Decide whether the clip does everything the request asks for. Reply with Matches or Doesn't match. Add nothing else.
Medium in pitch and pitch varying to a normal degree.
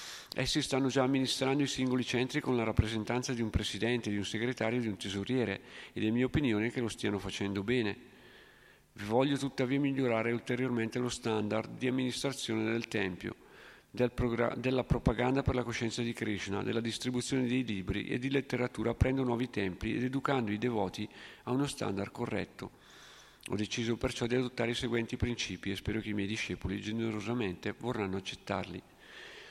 Doesn't match